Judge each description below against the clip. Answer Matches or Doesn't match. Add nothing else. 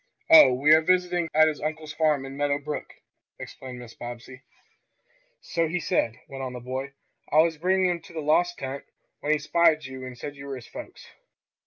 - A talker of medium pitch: Matches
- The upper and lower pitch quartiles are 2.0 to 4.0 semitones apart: Matches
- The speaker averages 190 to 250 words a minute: Matches